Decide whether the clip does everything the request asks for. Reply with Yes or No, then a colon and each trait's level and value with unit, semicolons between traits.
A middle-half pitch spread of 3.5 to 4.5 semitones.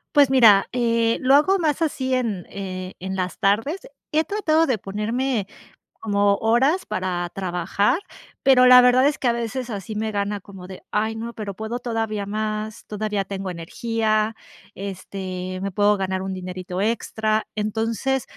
Yes: average, 4.1 semitones